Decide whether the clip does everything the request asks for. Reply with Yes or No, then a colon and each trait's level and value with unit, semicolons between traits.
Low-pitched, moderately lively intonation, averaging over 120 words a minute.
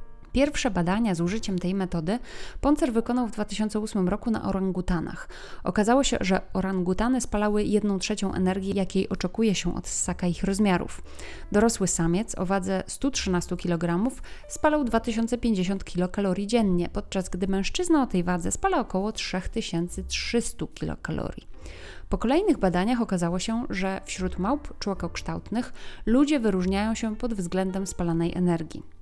No: high, 195 Hz; average, 3.8 semitones; average, 130 wpm